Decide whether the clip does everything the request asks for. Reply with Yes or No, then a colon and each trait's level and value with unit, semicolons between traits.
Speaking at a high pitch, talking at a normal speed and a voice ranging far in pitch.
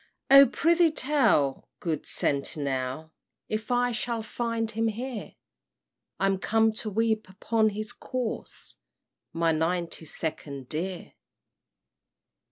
No: high, 215 Hz; slow, 105 wpm; wide, 6.3 semitones